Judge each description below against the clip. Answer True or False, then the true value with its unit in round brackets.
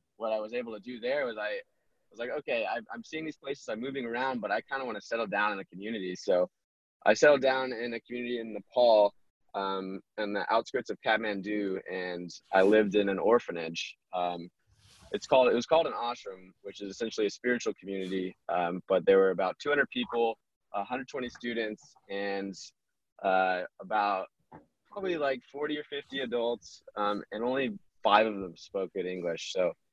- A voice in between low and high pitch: False (105 Hz)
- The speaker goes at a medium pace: True (190 wpm)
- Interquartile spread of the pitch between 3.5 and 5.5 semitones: True (4.1 semitones)